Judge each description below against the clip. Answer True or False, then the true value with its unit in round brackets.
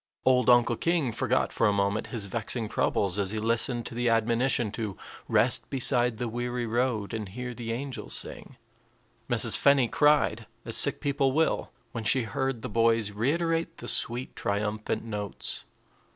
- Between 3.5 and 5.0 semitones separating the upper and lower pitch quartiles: False (2.9 semitones)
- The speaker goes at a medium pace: True (165 wpm)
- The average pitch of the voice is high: False (120 Hz)